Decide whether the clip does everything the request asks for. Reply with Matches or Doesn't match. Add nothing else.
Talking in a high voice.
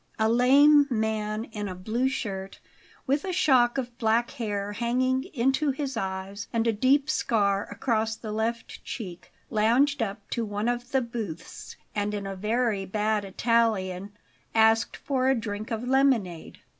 Matches